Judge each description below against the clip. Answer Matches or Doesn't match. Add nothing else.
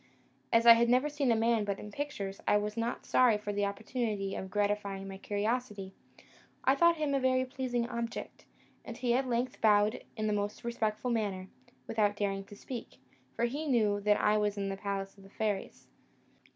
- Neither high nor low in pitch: Doesn't match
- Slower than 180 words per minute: Doesn't match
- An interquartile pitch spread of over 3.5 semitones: Doesn't match